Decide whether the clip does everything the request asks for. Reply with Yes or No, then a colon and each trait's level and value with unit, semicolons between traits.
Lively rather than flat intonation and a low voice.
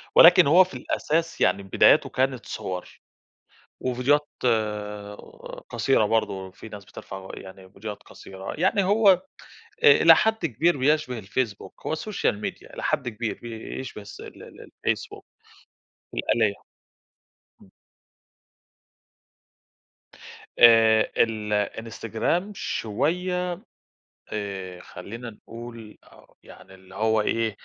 Yes: wide, 6.4 semitones; low, 115 Hz